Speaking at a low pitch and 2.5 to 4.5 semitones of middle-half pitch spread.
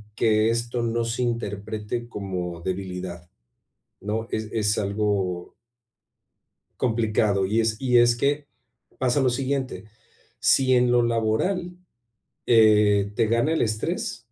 Yes: low, 110 Hz; average, 2.8 semitones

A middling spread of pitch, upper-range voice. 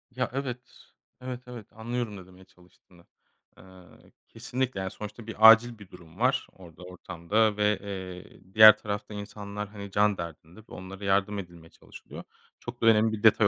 No: average, 3.2 semitones; low, 105 Hz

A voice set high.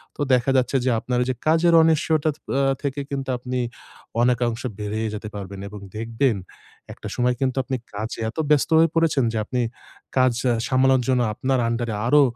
No: low, 130 Hz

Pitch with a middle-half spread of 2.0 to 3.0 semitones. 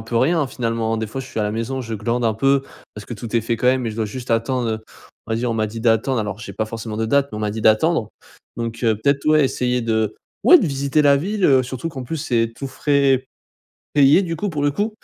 No: average, 3.8 semitones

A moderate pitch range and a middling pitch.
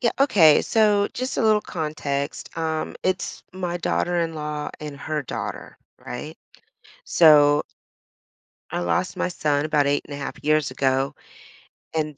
Yes: average, 3.3 semitones; medium, 155 Hz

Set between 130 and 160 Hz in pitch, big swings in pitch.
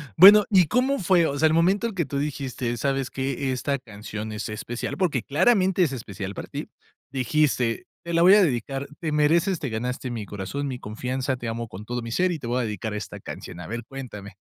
Yes: low, 135 Hz; wide, 6.1 semitones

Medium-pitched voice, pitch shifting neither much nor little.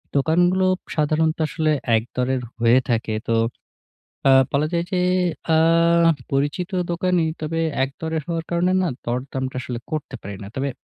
Yes: medium, 155 Hz; average, 4.5 semitones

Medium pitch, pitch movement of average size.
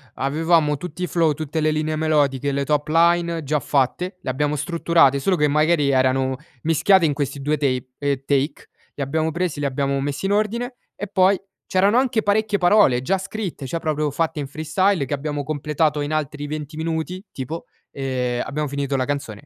Yes: medium, 150 Hz; average, 3.2 semitones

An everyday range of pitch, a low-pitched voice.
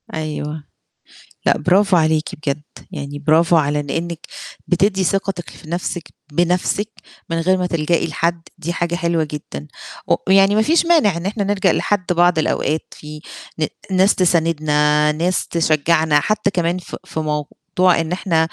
No: average, 3.3 semitones; medium, 170 Hz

